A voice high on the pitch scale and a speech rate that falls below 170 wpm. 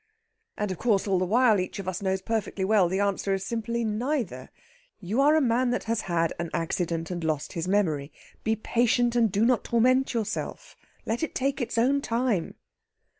No: high, 215 Hz; average, 195 wpm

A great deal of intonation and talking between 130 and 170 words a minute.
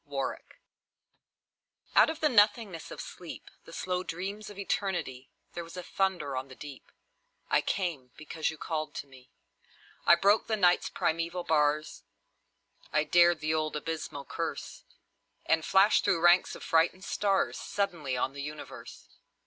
No: average, 4.0 semitones; average, 155 wpm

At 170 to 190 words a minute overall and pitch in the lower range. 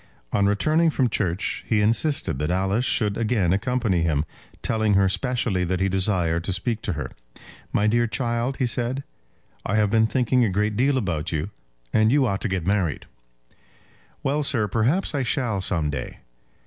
Yes: average, 175 wpm; low, 105 Hz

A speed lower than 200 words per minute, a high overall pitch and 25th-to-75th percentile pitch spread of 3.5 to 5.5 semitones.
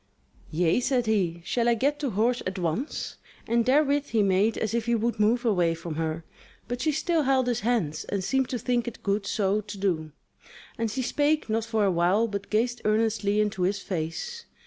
No: fast, 205 wpm; high, 220 Hz; average, 4.0 semitones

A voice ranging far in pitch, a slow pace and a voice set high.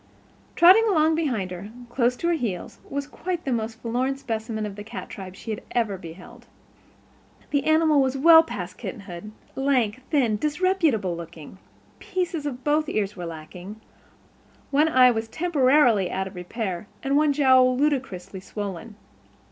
No: wide, 6.7 semitones; average, 155 wpm; high, 245 Hz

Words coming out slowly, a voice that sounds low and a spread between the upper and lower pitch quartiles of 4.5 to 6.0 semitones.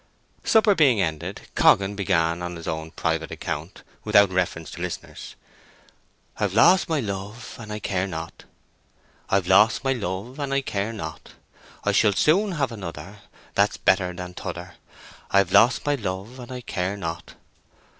No: average, 155 wpm; low, 100 Hz; average, 5.2 semitones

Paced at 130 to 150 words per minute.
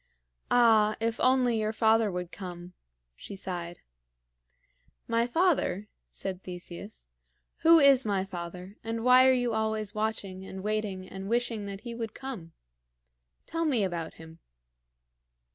Yes: slow, 135 wpm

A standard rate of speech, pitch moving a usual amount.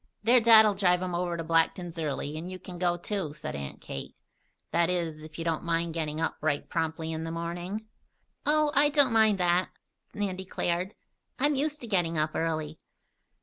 Yes: average, 190 wpm; average, 3.9 semitones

